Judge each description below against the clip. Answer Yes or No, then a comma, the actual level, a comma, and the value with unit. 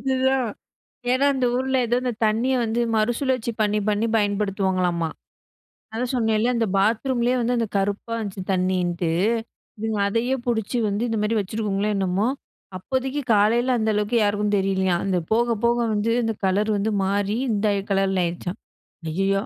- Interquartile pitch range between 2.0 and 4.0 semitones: Yes, average, 3.4 semitones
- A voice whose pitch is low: No, high, 215 Hz